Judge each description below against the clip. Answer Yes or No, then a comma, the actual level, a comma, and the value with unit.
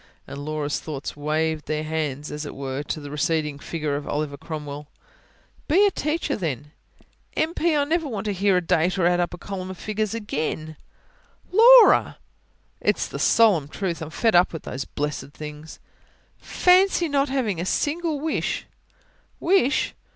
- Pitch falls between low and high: Yes, medium, 165 Hz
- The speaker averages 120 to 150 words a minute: No, average, 165 wpm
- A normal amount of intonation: No, wide, 7.5 semitones